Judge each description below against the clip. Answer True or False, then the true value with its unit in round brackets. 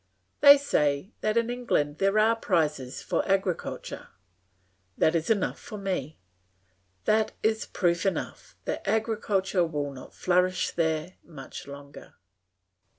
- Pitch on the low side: False (185 Hz)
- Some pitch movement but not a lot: False (5.8 semitones)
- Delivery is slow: True (125 wpm)